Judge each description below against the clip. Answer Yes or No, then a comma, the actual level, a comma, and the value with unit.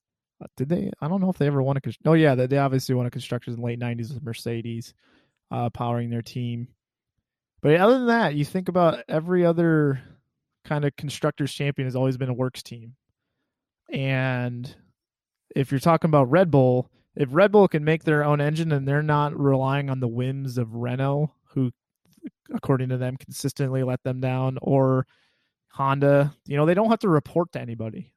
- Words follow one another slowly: No, average, 190 wpm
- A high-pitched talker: No, low, 135 Hz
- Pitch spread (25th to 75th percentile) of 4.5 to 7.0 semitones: No, average, 3.2 semitones